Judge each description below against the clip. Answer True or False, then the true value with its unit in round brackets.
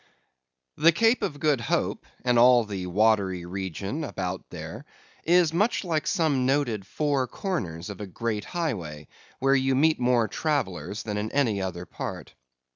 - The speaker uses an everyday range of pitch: False (7.7 semitones)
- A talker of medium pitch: False (120 Hz)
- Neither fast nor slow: True (165 wpm)